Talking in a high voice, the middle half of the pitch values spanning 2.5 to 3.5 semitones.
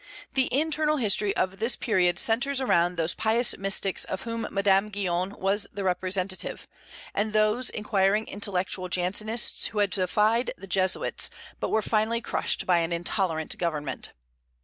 Yes: high, 200 Hz; average, 3.1 semitones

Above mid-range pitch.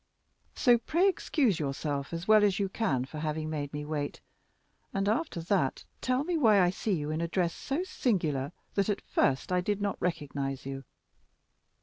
No: medium, 175 Hz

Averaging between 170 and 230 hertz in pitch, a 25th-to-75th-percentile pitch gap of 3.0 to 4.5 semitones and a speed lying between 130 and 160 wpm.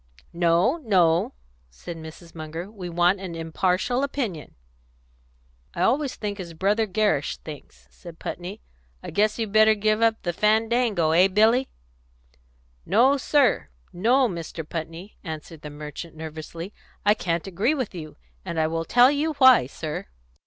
No: medium, 185 Hz; average, 5.2 semitones; average, 145 wpm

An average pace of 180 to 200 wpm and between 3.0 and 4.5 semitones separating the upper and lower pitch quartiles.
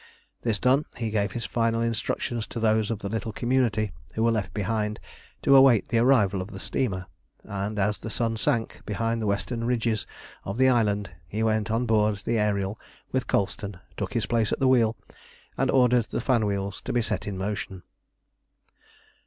No: average, 185 wpm; narrow, 2.4 semitones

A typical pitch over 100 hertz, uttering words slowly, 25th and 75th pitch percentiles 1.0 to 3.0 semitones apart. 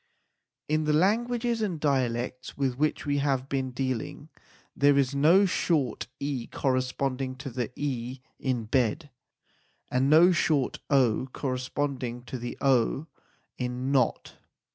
Yes: low, 135 Hz; slow, 130 wpm; narrow, 2.6 semitones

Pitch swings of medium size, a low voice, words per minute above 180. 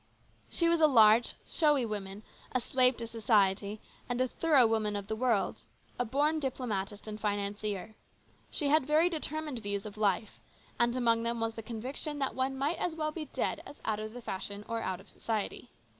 No: average, 4.5 semitones; high, 230 Hz; average, 190 wpm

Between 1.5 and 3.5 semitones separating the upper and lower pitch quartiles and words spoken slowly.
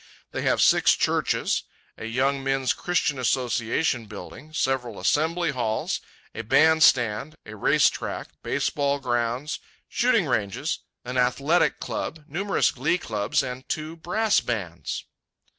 No: average, 5.1 semitones; slow, 125 wpm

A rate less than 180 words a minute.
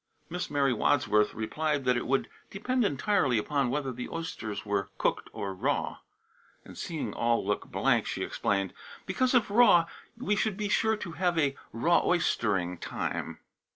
Yes: average, 165 wpm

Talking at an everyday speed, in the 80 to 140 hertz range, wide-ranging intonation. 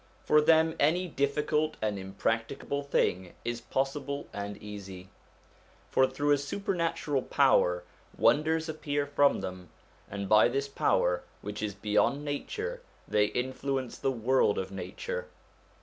No: slow, 130 wpm; low, 135 Hz; wide, 6.5 semitones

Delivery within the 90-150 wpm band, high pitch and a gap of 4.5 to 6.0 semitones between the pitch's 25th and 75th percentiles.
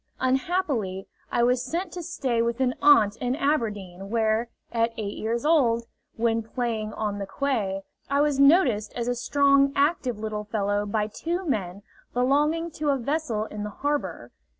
No: average, 165 wpm; high, 235 Hz; average, 4.8 semitones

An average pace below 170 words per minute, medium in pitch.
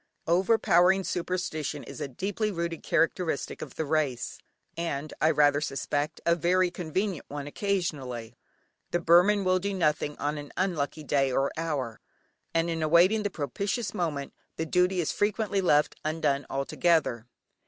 Yes: average, 145 wpm; medium, 165 Hz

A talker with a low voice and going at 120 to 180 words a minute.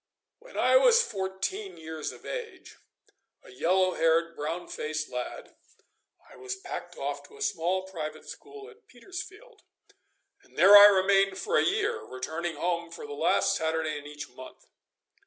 No: high, 190 Hz; average, 155 wpm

